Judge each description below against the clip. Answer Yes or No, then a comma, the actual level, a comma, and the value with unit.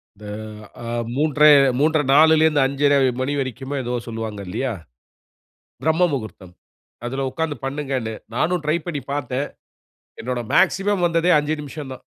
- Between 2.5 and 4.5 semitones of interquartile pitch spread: Yes, average, 3.5 semitones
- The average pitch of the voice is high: No, medium, 145 Hz